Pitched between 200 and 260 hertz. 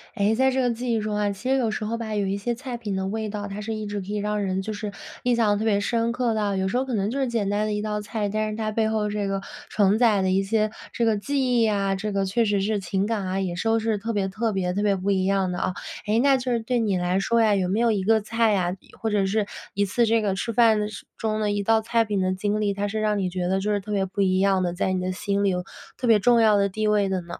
Yes: high, 210 Hz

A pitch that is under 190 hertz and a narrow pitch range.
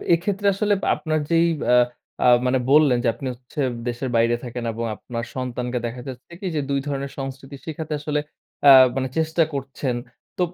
No: low, 135 Hz; average, 3.8 semitones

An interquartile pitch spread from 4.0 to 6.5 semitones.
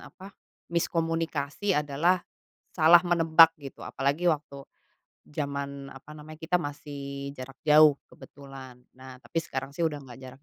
No: average, 2.9 semitones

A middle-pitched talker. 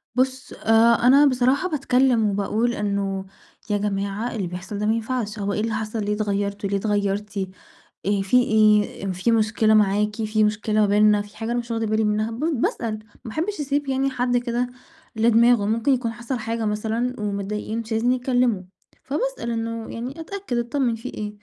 No: high, 225 Hz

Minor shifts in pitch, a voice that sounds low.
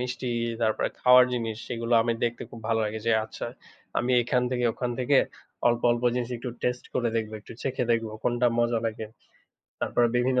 Yes: narrow, 1.5 semitones; low, 120 Hz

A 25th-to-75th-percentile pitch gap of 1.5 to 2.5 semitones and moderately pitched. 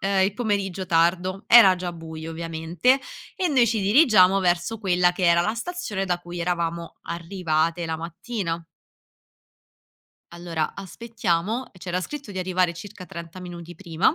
No: average, 2.9 semitones; medium, 180 Hz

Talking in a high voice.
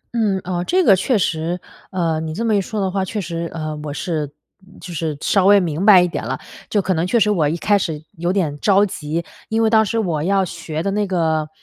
No: medium, 180 Hz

